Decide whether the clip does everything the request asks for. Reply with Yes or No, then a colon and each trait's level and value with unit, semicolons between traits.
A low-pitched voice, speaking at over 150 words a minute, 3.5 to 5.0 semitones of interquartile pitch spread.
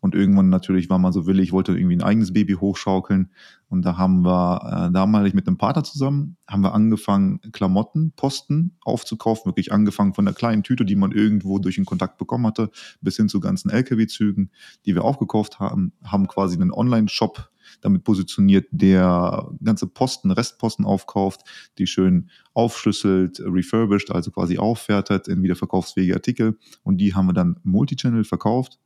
Yes: low, 100 Hz; average, 165 wpm; average, 3.8 semitones